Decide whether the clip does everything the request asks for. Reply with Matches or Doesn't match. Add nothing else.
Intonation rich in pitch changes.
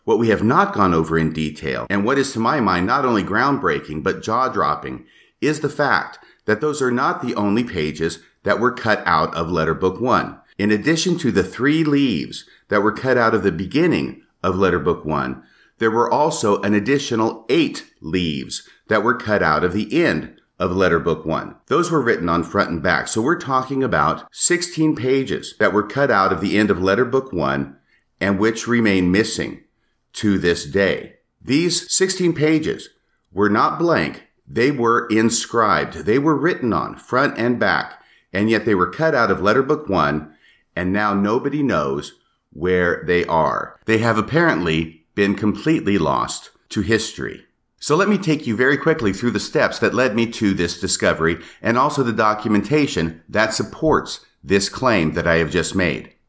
Matches